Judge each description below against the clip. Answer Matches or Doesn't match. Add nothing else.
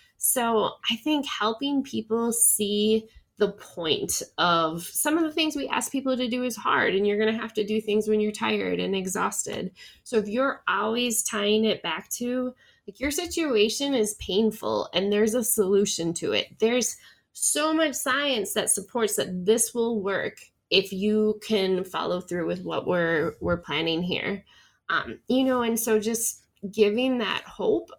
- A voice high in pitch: Matches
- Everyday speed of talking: Matches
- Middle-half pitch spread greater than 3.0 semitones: Matches